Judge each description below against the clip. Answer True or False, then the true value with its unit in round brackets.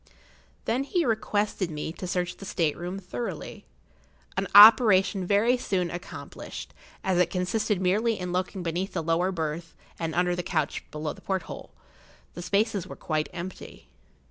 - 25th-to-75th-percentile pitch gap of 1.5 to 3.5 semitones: True (2.9 semitones)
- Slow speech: False (155 wpm)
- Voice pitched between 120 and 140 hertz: False (180 Hz)